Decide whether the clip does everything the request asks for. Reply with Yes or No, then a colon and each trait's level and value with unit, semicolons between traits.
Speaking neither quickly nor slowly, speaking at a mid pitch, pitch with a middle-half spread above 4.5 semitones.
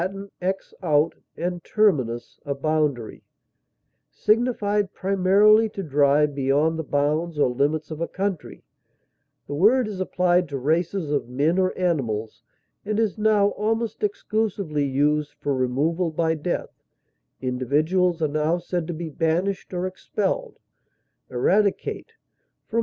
No: slow, 130 wpm; medium, 165 Hz; average, 5.0 semitones